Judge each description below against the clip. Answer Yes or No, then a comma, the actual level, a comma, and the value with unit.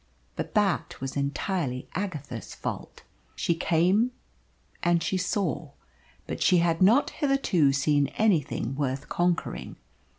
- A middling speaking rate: No, slow, 120 wpm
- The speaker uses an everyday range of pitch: Yes, average, 5.0 semitones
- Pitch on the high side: No, medium, 165 Hz